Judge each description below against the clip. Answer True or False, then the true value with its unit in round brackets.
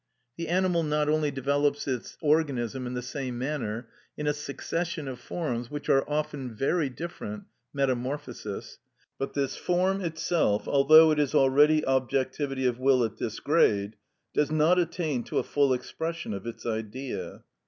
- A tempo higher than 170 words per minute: False (155 wpm)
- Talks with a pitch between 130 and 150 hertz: True (140 Hz)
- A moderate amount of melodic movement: True (3.6 semitones)